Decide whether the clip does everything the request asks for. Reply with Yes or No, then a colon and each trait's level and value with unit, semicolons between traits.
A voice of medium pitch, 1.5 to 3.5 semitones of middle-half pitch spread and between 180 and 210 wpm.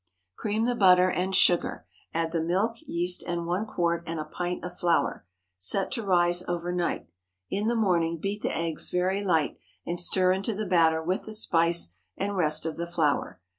Yes: medium, 175 Hz; narrow, 2.5 semitones; average, 190 wpm